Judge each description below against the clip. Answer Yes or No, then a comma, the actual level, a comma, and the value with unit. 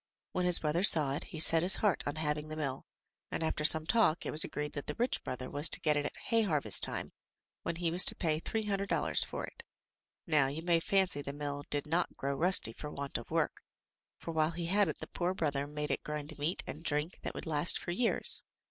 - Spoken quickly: Yes, fast, 245 wpm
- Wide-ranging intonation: No, average, 3.0 semitones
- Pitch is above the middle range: No, medium, 155 Hz